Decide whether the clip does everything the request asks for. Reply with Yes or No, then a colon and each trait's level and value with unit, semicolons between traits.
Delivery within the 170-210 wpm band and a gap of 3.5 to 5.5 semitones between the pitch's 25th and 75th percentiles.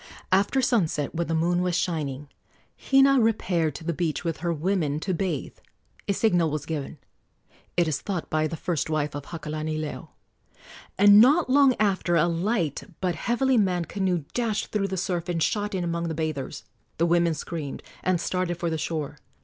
Yes: average, 180 wpm; average, 3.9 semitones